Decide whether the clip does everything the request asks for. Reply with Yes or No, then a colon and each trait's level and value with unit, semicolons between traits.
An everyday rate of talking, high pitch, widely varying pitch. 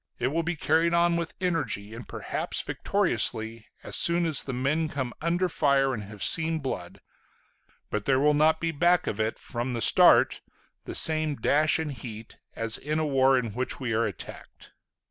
No: average, 185 wpm; medium, 140 Hz; wide, 5.7 semitones